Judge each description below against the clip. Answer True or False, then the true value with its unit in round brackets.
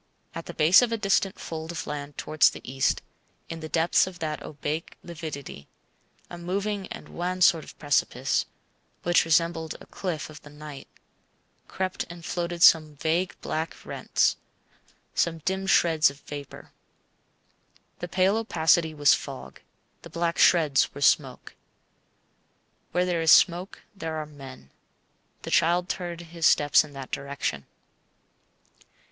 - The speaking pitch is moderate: True (165 Hz)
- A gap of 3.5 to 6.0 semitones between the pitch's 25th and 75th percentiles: False (3.0 semitones)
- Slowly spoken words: False (145 wpm)